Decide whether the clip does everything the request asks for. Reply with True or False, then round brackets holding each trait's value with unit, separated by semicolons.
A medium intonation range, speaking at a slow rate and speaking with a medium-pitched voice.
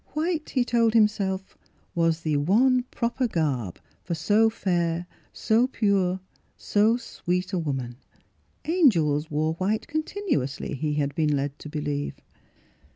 False (7.1 semitones; 130 wpm; 180 Hz)